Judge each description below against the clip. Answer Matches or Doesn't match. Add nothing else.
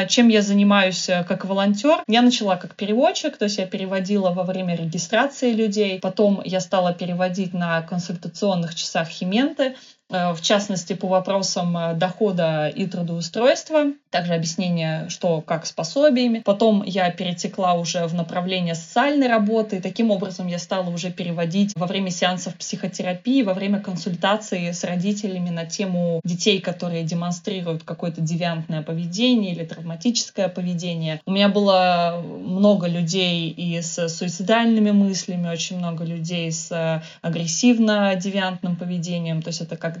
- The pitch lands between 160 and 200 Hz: Matches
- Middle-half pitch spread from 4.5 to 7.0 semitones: Doesn't match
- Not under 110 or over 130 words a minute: Doesn't match